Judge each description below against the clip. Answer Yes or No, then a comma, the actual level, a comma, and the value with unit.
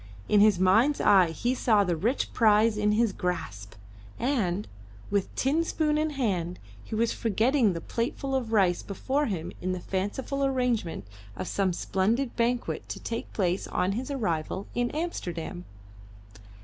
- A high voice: Yes, high, 215 Hz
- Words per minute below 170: Yes, average, 160 wpm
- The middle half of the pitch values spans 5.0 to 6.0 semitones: Yes, average, 5.3 semitones